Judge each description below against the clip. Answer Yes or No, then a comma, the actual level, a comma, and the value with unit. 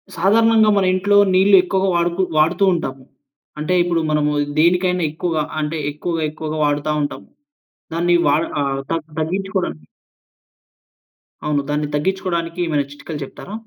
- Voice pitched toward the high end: No, medium, 165 Hz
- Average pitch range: Yes, average, 3.6 semitones